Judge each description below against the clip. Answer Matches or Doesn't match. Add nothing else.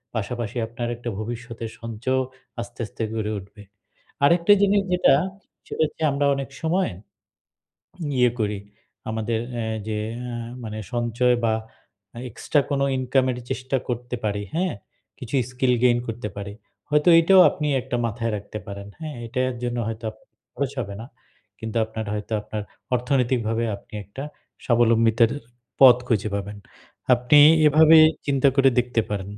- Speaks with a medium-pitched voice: Doesn't match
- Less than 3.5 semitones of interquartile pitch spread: Matches